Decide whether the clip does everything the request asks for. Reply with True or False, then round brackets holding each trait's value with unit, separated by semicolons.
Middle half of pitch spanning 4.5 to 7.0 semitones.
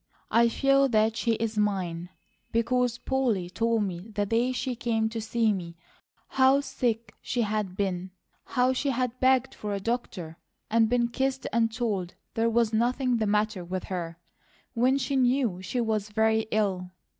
False (3.4 semitones)